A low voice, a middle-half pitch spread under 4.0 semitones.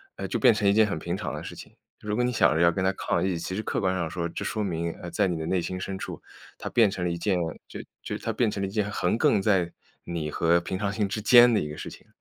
Yes: very low, 95 Hz; average, 3.6 semitones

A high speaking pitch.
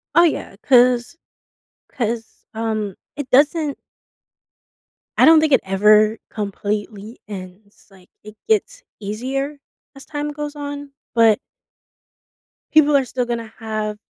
Yes: high, 235 Hz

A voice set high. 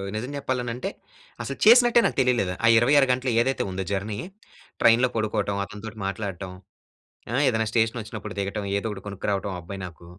No: low, 110 Hz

